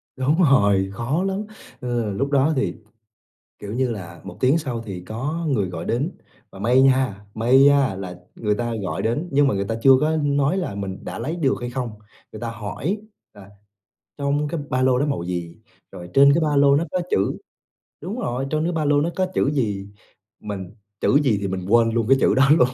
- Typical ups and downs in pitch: No, wide, 5.9 semitones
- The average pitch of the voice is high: No, low, 130 Hz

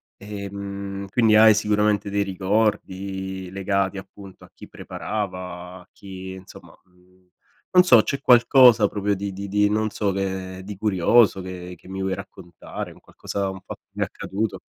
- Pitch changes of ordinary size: No, narrow, 1.8 semitones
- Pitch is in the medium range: No, low, 100 Hz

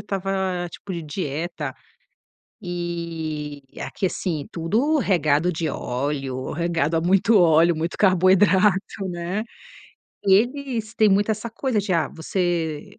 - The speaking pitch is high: No, medium, 175 Hz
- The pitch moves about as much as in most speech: Yes, average, 3.5 semitones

